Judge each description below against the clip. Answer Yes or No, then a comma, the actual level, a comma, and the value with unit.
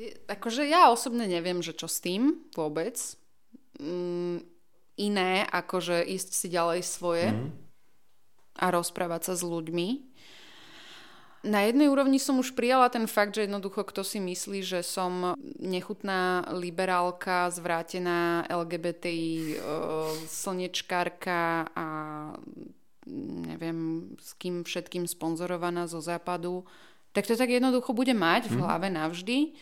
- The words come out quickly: No, average, 115 wpm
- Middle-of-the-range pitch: Yes, medium, 180 Hz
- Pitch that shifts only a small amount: No, average, 3.4 semitones